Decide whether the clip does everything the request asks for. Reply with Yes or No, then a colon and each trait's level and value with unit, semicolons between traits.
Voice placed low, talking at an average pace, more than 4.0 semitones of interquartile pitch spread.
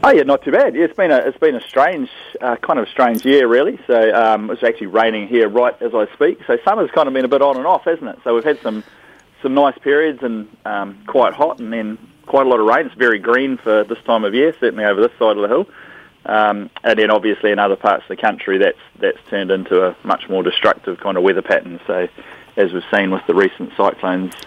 No: low, 115 Hz; fast, 260 wpm; average, 4.9 semitones